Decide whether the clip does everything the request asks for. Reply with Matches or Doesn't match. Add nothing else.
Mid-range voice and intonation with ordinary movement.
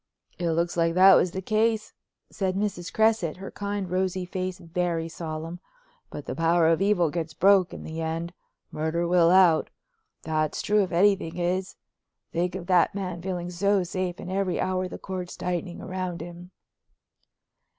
Doesn't match